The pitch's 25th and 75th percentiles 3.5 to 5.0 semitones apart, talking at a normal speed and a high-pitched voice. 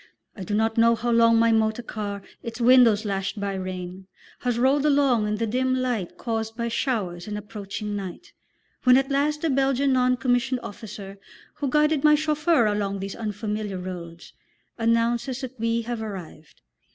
Yes: average, 3.9 semitones; average, 170 wpm; high, 230 Hz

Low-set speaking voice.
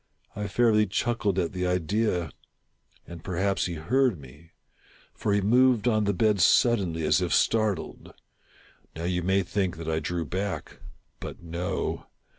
Yes: very low, 95 Hz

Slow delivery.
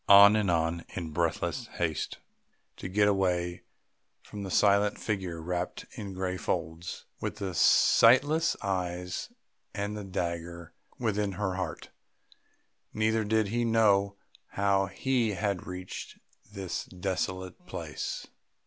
Yes: slow, 120 wpm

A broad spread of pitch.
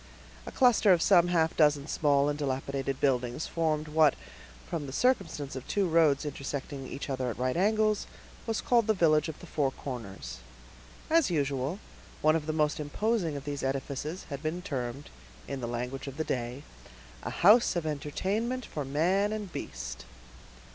No: average, 4.6 semitones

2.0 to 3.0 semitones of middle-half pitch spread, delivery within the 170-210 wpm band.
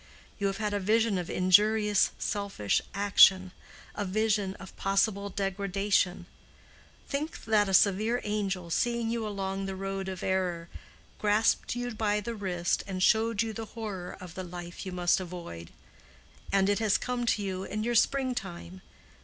No: narrow, 2.6 semitones; average, 160 wpm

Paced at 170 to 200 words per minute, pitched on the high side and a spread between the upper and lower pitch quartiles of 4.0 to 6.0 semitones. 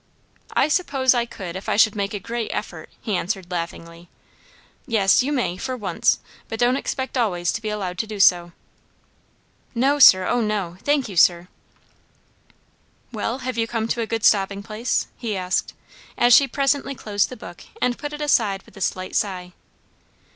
Yes: average, 180 wpm; high, 215 Hz; average, 4.8 semitones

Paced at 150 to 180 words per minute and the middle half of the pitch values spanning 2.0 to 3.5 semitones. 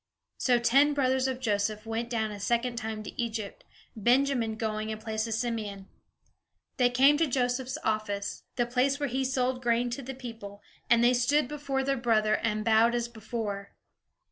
Yes: average, 175 wpm; average, 2.9 semitones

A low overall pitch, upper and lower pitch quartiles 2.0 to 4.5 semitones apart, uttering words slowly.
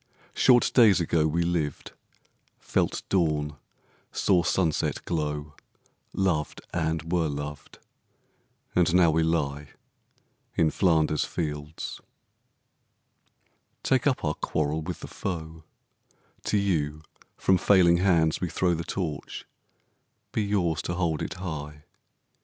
Yes: very low, 80 Hz; average, 2.8 semitones; slow, 115 wpm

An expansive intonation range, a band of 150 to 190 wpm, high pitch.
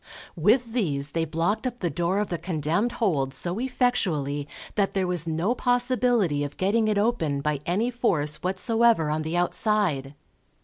No: wide, 6.8 semitones; average, 165 wpm; medium, 180 Hz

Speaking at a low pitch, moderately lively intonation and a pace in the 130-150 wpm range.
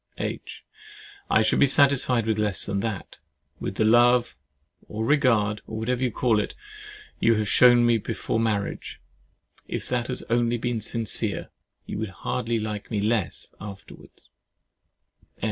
No: low, 115 Hz; narrow, 2.3 semitones; average, 145 wpm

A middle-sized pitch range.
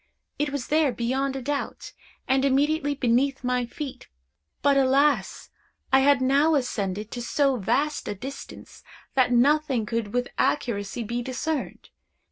Yes: average, 3.0 semitones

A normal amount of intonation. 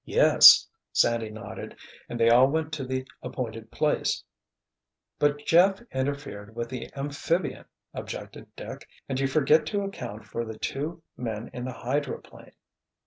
Yes: average, 3.9 semitones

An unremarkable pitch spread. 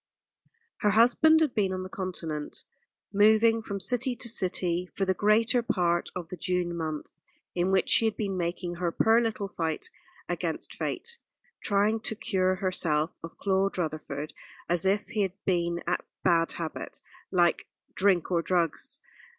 Yes: average, 3.6 semitones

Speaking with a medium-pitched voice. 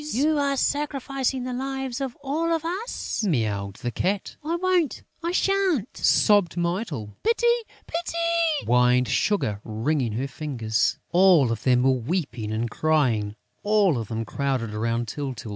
Yes: medium, 175 Hz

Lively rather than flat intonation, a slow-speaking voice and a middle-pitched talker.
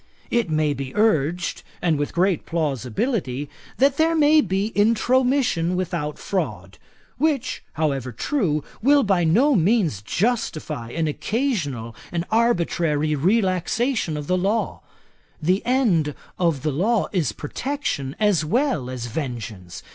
Yes: wide, 7.7 semitones; slow, 125 wpm; medium, 175 Hz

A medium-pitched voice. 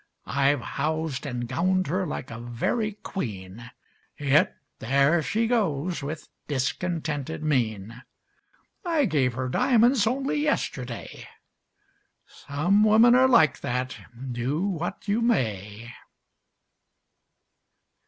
Yes: medium, 150 Hz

